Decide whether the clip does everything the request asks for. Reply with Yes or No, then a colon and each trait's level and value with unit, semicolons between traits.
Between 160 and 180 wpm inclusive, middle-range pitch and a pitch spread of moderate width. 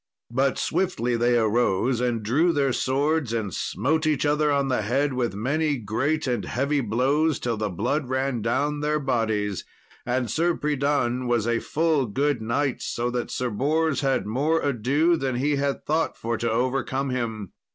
No: average, 170 wpm; low, 130 Hz; average, 3.7 semitones